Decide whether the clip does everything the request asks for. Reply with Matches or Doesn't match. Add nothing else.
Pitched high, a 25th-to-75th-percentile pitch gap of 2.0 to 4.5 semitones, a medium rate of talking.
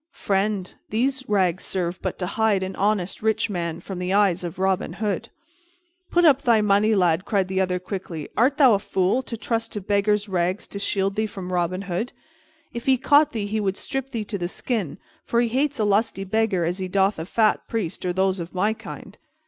Doesn't match